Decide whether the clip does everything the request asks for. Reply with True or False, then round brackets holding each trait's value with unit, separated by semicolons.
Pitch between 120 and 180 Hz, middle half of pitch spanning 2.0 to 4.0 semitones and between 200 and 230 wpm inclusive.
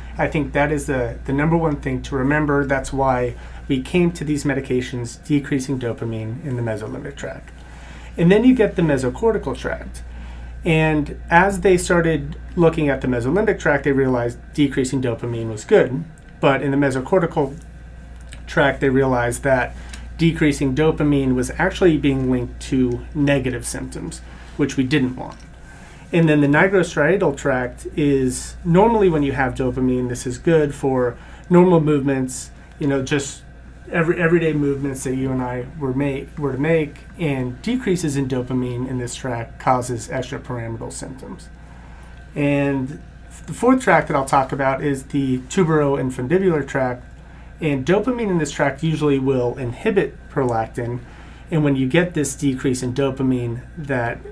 False (140 Hz; 3.5 semitones; 155 wpm)